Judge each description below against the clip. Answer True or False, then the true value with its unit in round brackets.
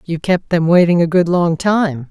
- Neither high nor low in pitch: True (170 Hz)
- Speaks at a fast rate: True (230 wpm)